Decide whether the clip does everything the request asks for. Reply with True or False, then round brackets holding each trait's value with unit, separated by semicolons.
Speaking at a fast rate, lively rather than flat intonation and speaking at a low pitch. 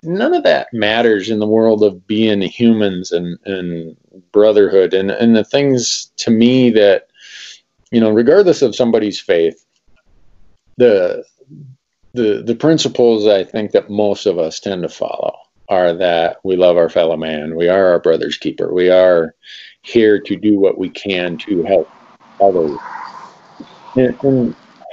False (155 wpm; 6.1 semitones; 110 Hz)